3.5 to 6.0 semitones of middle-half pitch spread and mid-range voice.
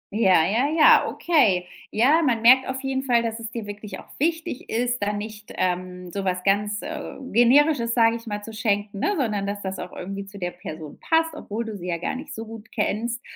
No: average, 4.3 semitones; high, 220 Hz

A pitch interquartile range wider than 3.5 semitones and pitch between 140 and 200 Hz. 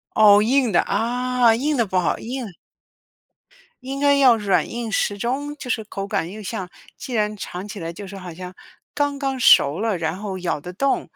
No: average, 5.1 semitones; high, 215 Hz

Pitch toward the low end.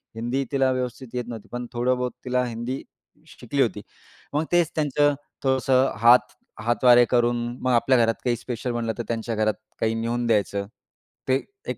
Yes: low, 120 Hz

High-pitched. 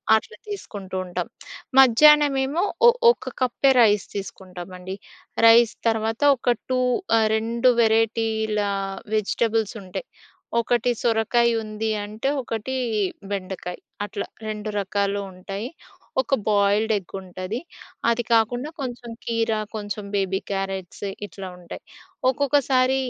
Yes: high, 220 Hz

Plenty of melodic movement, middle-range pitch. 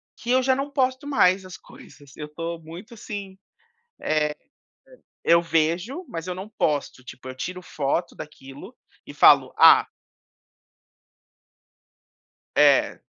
Yes: wide, 6.1 semitones; medium, 180 Hz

